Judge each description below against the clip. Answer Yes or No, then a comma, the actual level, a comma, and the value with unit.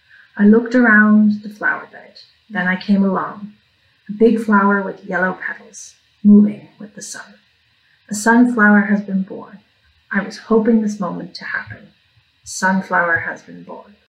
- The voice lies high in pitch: Yes, high, 205 Hz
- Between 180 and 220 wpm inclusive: No, average, 160 wpm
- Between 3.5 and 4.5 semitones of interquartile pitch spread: No, average, 2.7 semitones